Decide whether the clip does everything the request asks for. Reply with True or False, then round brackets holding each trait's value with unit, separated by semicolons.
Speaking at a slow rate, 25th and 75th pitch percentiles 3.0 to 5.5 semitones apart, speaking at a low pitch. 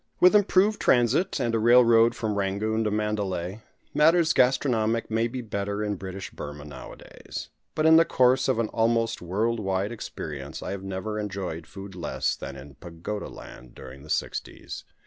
False (165 wpm; 3.9 semitones; 105 Hz)